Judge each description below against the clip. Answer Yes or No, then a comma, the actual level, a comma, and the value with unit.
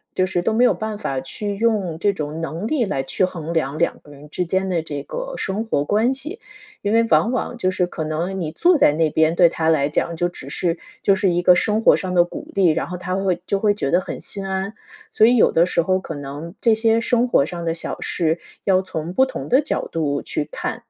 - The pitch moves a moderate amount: Yes, average, 4.6 semitones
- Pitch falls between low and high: Yes, medium, 180 Hz